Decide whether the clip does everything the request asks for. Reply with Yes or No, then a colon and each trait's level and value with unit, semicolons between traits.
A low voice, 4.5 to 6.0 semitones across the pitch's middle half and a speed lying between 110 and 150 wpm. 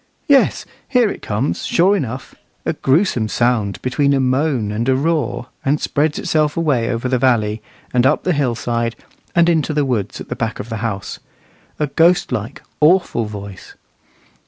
No: low, 130 Hz; average, 4.9 semitones; average, 170 wpm